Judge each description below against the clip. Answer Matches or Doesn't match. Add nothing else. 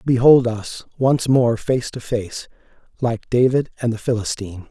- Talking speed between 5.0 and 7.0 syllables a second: Doesn't match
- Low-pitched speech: Matches